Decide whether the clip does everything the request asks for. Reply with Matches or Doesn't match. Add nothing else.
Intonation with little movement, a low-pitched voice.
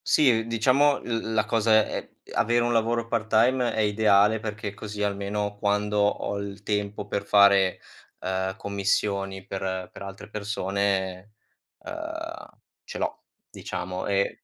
Matches